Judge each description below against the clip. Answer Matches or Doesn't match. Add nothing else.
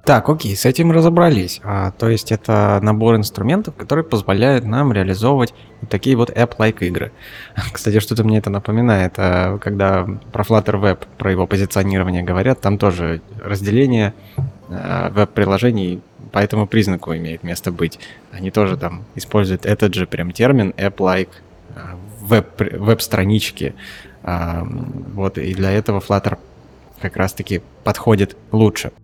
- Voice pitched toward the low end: Matches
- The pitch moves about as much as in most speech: Matches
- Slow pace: Doesn't match